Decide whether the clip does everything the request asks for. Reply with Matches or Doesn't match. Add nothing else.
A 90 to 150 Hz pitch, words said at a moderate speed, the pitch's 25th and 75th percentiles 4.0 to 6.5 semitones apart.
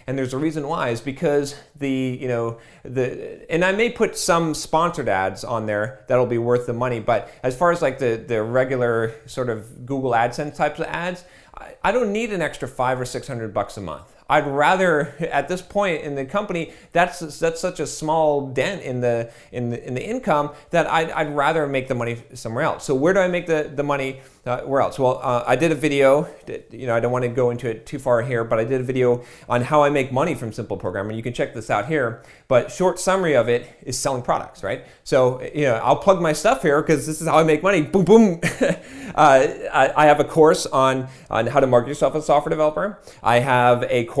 Doesn't match